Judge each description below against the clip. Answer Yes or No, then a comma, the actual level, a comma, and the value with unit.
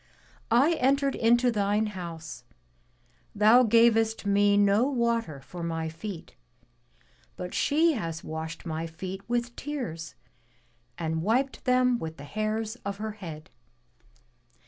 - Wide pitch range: Yes, wide, 6.3 semitones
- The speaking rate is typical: No, slow, 125 wpm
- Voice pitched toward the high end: Yes, high, 210 Hz